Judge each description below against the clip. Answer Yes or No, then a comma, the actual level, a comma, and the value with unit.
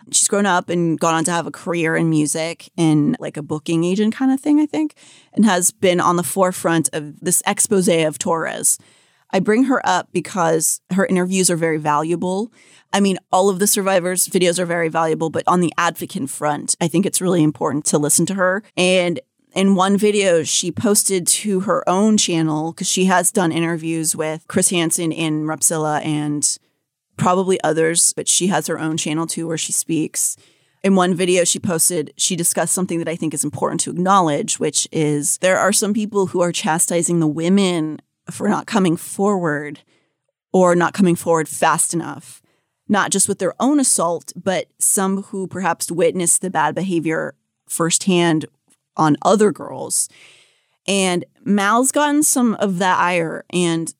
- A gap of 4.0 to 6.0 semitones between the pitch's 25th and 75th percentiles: No, average, 2.9 semitones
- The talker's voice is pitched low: No, medium, 175 Hz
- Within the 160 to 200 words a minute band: Yes, average, 180 wpm